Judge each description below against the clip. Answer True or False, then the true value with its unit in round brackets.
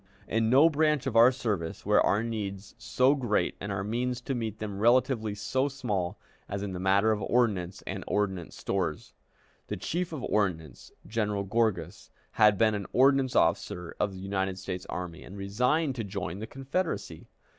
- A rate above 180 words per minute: False (175 wpm)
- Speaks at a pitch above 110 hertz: False (105 Hz)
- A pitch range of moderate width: True (4.3 semitones)